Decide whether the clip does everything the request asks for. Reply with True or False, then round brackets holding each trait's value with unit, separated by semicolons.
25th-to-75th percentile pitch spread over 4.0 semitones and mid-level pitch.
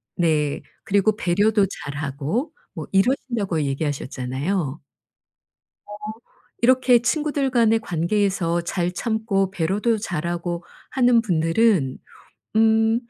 False (5.5 semitones; 195 Hz)